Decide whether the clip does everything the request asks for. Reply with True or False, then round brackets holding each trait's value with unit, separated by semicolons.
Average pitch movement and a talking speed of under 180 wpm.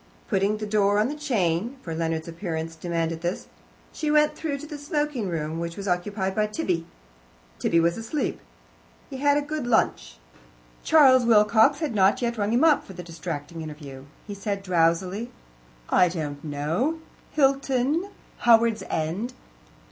False (7.6 semitones; 160 wpm)